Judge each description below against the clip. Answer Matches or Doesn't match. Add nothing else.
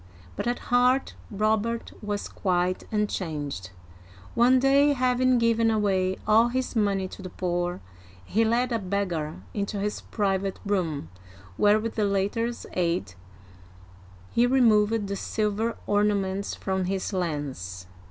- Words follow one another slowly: Matches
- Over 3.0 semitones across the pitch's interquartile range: Matches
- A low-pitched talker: Doesn't match